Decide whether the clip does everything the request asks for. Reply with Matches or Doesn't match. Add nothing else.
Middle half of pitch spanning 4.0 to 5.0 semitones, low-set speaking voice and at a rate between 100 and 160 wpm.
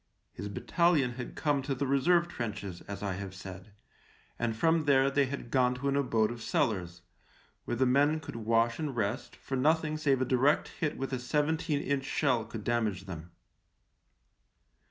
Doesn't match